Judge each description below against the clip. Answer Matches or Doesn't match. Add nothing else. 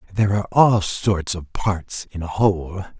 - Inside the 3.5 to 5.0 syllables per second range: Matches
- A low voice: Matches